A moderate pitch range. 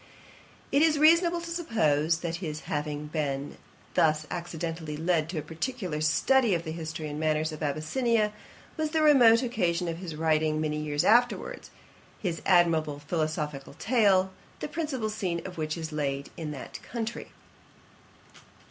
No: wide, 6.6 semitones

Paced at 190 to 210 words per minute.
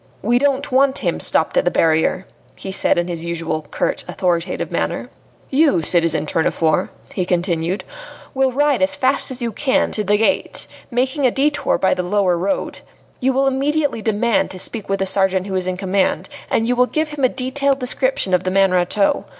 Yes: average, 195 wpm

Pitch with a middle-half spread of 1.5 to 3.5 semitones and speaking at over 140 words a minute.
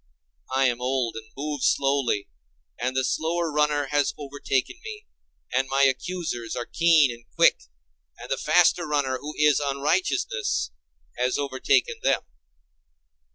No: average, 2.8 semitones; slow, 135 wpm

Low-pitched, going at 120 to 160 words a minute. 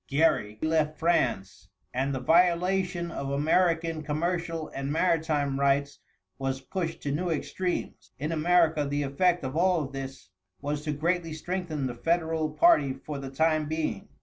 No: medium, 155 Hz; average, 150 wpm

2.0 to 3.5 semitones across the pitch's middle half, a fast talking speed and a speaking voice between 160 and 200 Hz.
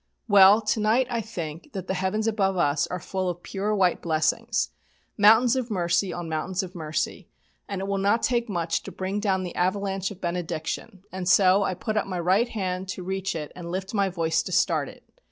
Yes: average, 2.8 semitones; fast, 210 wpm; high, 190 Hz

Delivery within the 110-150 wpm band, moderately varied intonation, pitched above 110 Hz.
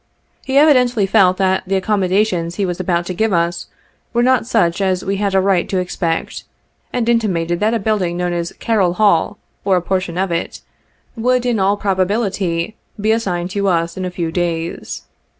No: average, 190 wpm; average, 3.6 semitones; high, 190 Hz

